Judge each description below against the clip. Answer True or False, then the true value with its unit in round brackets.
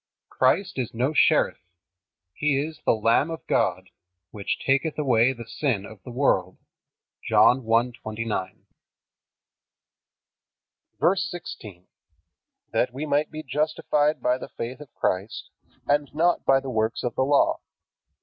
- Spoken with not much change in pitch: False (4.7 semitones)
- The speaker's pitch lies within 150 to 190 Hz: False (130 Hz)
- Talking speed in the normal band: False (130 wpm)